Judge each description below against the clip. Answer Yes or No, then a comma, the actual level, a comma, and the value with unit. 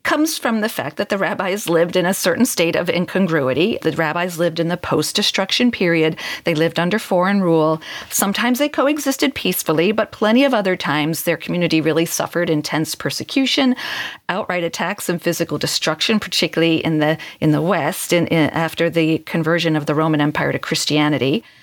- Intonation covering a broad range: No, average, 4.0 semitones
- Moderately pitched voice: Yes, medium, 170 Hz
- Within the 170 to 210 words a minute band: Yes, average, 180 wpm